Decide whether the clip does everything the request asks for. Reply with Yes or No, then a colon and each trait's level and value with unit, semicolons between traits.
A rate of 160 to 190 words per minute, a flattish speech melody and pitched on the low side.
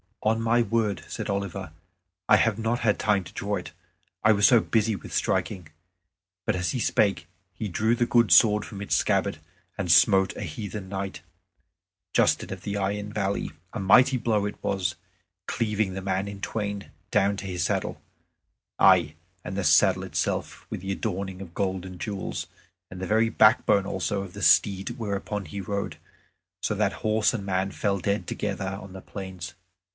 Yes: average, 180 wpm; narrow, 2.0 semitones; low, 100 Hz